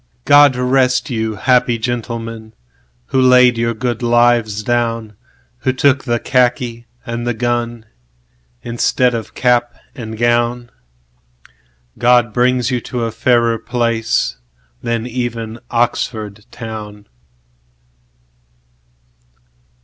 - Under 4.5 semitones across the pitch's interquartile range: Yes, average, 2.7 semitones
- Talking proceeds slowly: Yes, slow, 90 wpm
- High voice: No, low, 115 Hz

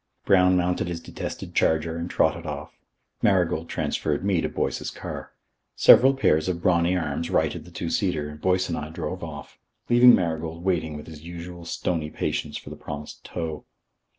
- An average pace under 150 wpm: No, average, 175 wpm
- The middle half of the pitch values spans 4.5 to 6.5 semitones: No, narrow, 2.6 semitones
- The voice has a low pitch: Yes, very low, 85 Hz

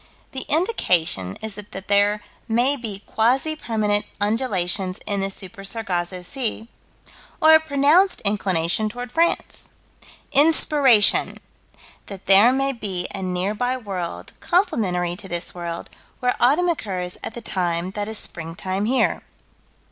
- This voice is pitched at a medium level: No, high, 210 Hz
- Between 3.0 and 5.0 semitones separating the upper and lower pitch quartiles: No, wide, 5.5 semitones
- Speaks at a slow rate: Yes, slow, 130 wpm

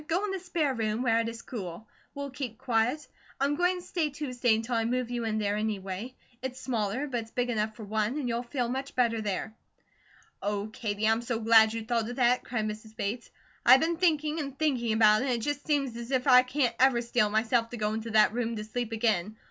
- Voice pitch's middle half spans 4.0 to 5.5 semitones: No, average, 3.1 semitones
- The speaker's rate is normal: No, fast, 235 wpm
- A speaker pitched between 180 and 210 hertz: No, high, 235 Hz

